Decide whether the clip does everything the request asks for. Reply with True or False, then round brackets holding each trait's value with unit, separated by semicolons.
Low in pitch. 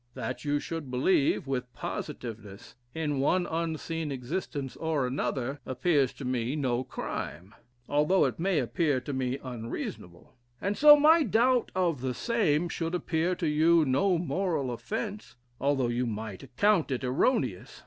False (145 Hz)